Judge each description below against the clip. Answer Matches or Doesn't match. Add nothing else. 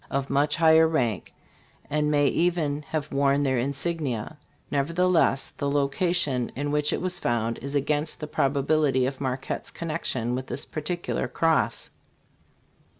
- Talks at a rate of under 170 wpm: Matches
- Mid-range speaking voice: Matches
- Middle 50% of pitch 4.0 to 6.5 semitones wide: Doesn't match